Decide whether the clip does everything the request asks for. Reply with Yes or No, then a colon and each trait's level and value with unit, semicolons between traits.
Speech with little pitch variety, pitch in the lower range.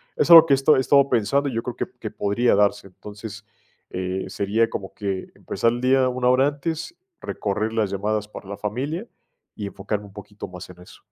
No: average, 4.5 semitones; low, 110 Hz